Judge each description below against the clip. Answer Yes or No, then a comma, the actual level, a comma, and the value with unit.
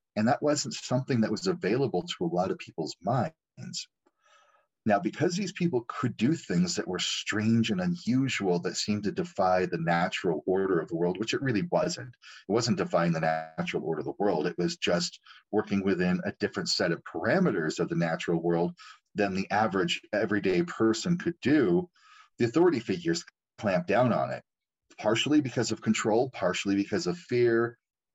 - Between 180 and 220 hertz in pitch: No, low, 105 Hz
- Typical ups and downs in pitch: No, wide, 7.6 semitones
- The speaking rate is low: No, average, 180 wpm